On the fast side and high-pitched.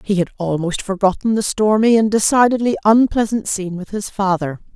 No: average, 165 wpm; high, 205 Hz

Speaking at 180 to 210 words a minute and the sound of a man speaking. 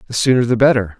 No: fast, 240 wpm; male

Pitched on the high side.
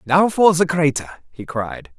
No: medium, 155 Hz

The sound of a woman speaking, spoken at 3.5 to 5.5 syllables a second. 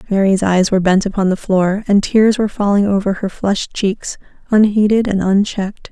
Yes: female; 5.4 syllables/s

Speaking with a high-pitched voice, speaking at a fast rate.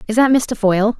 Yes: high, 225 Hz; fast, 240 wpm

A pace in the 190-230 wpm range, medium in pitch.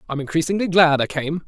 Yes: fast, 205 wpm; medium, 160 Hz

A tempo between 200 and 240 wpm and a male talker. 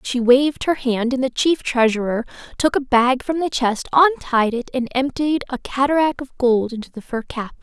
No: fast, 205 wpm; female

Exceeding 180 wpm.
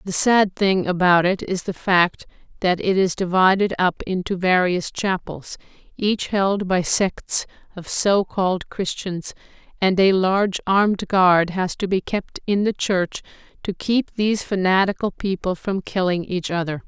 No: average, 155 wpm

